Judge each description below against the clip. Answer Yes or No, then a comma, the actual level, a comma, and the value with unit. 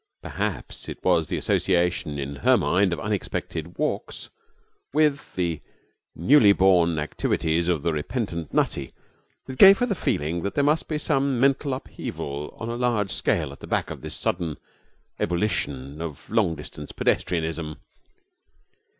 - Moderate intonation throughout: No, wide, 7.8 semitones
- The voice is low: Yes, very low, 90 Hz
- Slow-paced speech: No, average, 150 wpm